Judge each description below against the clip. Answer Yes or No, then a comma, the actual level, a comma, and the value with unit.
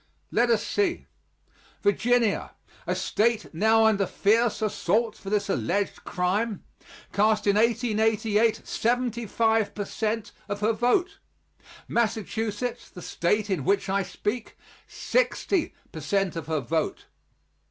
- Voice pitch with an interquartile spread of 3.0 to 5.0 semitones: No, narrow, 2.5 semitones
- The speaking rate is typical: No, slow, 125 wpm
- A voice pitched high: Yes, high, 215 Hz